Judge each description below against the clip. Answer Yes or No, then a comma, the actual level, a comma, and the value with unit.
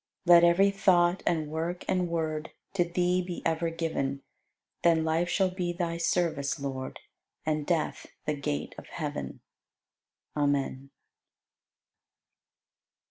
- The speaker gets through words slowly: Yes, slow, 120 wpm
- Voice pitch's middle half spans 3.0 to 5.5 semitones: No, narrow, 2.5 semitones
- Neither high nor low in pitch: Yes, medium, 165 Hz